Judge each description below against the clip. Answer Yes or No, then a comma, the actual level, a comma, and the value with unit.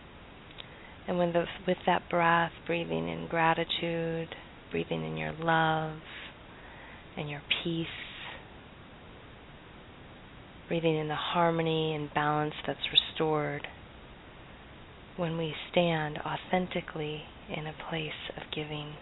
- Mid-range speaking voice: Yes, medium, 160 Hz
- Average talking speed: No, slow, 100 wpm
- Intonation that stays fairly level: Yes, narrow, 2.0 semitones